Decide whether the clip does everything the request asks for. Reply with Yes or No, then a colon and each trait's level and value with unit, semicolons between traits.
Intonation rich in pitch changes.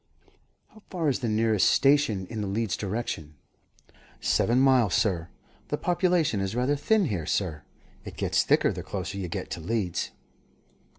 Yes: wide, 6.3 semitones